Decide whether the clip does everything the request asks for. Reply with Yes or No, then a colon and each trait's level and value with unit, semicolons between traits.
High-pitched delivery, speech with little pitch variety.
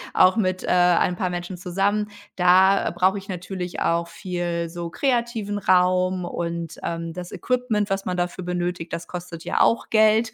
No: medium, 180 Hz; narrow, 2.1 semitones